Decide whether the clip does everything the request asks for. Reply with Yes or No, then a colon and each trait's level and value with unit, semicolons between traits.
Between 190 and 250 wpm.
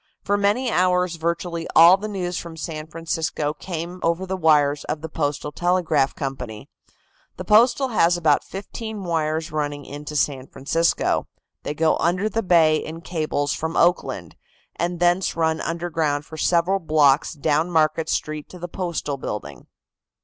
No: average, 155 wpm